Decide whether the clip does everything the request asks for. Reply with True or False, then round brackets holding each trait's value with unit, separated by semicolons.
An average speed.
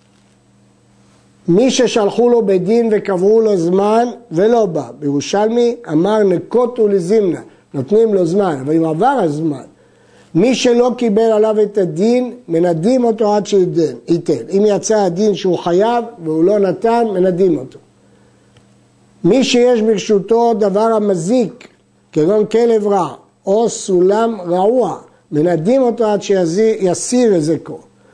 True (125 wpm)